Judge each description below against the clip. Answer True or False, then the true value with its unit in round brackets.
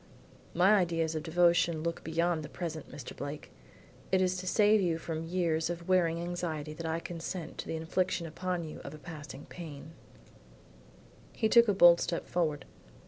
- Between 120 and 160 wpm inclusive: False (175 wpm)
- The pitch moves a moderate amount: False (2.0 semitones)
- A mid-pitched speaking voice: True (170 Hz)